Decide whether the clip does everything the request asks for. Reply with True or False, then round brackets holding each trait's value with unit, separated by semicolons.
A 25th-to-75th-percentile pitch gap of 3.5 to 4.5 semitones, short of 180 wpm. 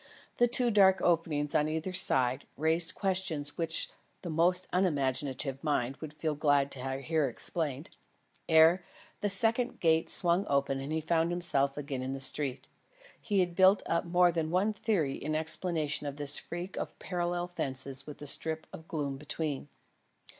True (3.8 semitones; 165 wpm)